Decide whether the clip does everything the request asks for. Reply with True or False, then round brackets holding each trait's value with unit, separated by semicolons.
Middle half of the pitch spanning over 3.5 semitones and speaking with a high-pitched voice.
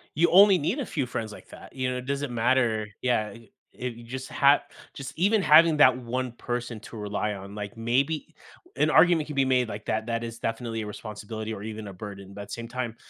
False (4.0 semitones; 120 Hz)